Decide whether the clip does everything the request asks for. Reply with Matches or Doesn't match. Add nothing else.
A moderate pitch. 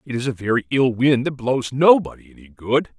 Doesn't match